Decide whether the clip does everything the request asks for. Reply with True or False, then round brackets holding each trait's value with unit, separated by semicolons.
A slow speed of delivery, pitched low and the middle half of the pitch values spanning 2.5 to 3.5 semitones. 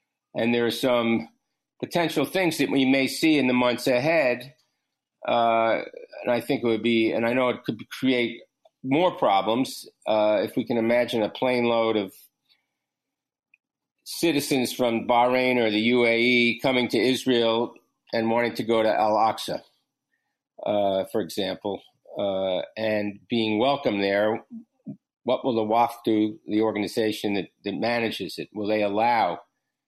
False (155 wpm; 115 Hz; 2.8 semitones)